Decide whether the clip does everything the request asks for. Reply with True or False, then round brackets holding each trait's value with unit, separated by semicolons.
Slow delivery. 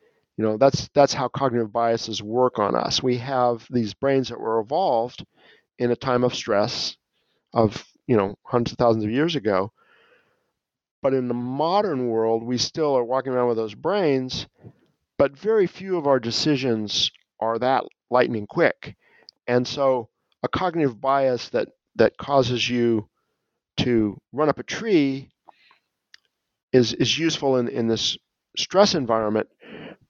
False (150 wpm)